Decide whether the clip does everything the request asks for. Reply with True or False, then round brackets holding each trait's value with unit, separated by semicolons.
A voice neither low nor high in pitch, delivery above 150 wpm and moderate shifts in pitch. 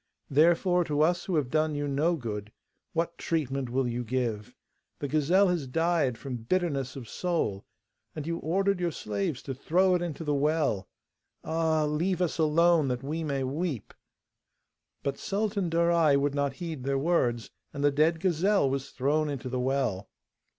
True (150 Hz; 170 wpm; 4.1 semitones)